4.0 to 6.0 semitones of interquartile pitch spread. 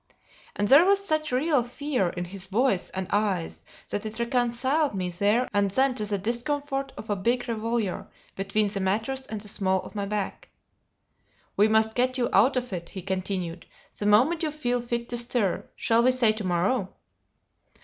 Yes: average, 4.4 semitones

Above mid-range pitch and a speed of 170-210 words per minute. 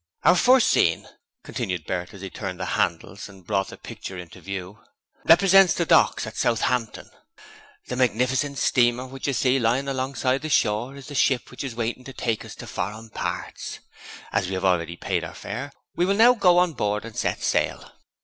No: low, 120 Hz; average, 195 wpm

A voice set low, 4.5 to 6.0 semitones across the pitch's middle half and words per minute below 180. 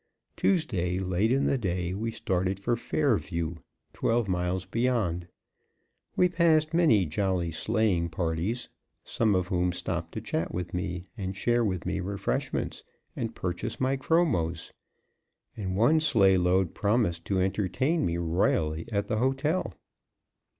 Yes: very low, 95 Hz; average, 5.3 semitones; slow, 135 wpm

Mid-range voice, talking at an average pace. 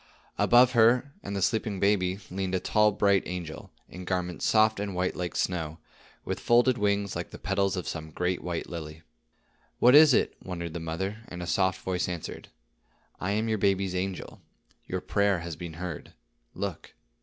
No: very low, 95 Hz; average, 180 wpm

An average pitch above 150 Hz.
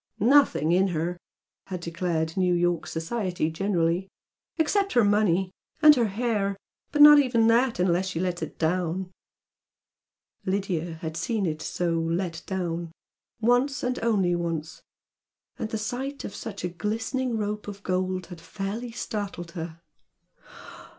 Yes: high, 190 Hz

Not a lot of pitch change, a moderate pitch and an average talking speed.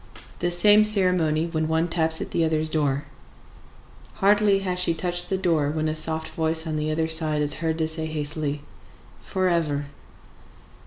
Yes: narrow, 2.1 semitones; medium, 160 Hz; average, 165 wpm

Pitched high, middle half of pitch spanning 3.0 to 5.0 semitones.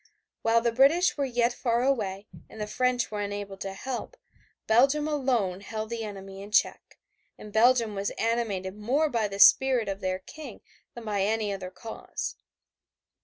Yes: high, 220 Hz; average, 3.9 semitones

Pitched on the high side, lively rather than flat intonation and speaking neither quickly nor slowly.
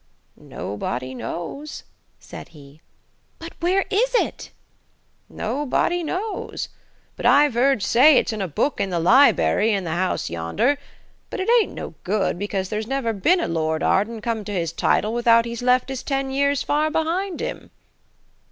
Yes: high, 235 Hz; wide, 7.6 semitones; average, 160 wpm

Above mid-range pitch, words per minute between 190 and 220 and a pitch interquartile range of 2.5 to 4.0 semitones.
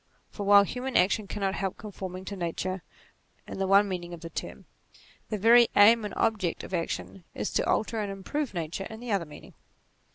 Yes: high, 195 Hz; average, 200 wpm; average, 2.8 semitones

